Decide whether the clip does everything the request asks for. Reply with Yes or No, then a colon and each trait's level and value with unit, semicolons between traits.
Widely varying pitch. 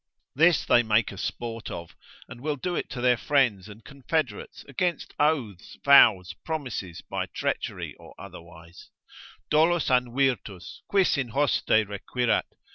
Yes: wide, 5.9 semitones